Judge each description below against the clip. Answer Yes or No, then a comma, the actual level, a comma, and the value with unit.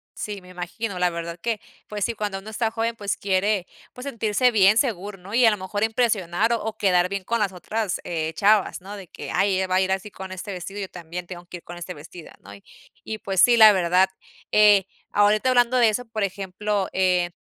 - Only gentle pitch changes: No, average, 3.1 semitones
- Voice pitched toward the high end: Yes, high, 200 Hz